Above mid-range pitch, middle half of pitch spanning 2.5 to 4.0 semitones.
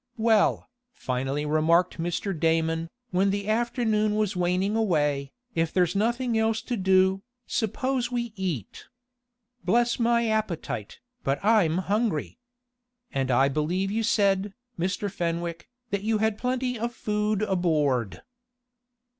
No: high, 195 Hz; average, 5.1 semitones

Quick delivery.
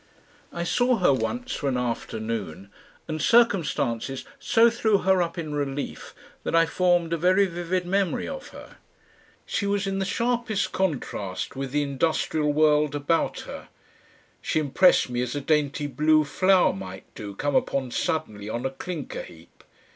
No: average, 160 wpm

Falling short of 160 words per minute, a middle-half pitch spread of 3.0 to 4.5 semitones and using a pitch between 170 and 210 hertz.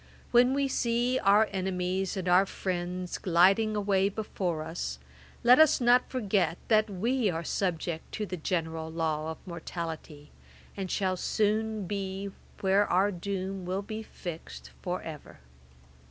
Yes: average, 140 wpm; average, 3.4 semitones; high, 190 Hz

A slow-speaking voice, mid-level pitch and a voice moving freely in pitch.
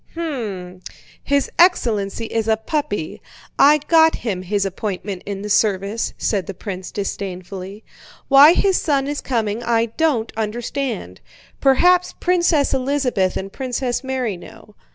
No: slow, 130 wpm; high, 225 Hz; wide, 6.0 semitones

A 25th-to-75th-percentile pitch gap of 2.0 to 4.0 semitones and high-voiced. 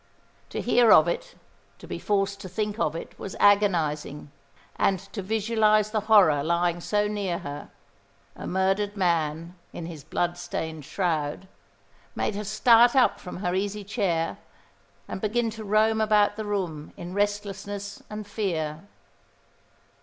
Yes: average, 3.6 semitones; high, 200 Hz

